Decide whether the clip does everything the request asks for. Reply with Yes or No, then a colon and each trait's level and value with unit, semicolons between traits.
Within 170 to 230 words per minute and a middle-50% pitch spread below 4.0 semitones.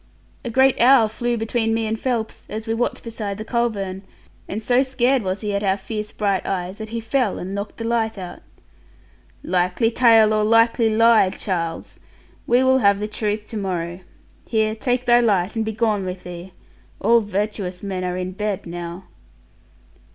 Yes: average, 180 wpm; average, 3.2 semitones